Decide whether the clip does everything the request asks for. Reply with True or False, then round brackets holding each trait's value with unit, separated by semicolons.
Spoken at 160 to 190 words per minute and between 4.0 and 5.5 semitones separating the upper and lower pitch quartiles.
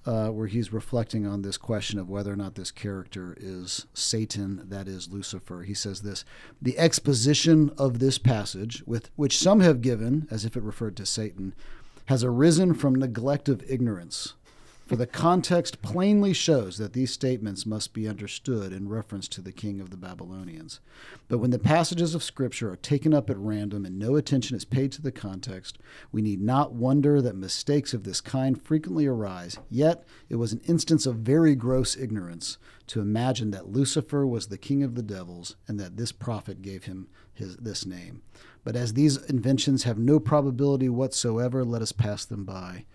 True (185 wpm; 5.1 semitones)